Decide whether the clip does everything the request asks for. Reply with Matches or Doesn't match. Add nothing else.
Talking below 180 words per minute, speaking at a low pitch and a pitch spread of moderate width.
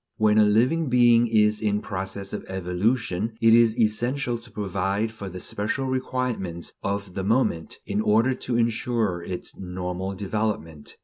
Matches